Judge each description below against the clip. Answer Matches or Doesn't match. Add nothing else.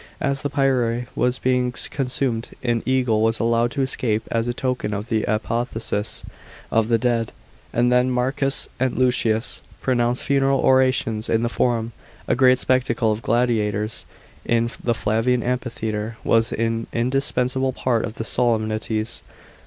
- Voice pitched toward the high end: Doesn't match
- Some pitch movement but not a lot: Doesn't match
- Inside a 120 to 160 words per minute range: Matches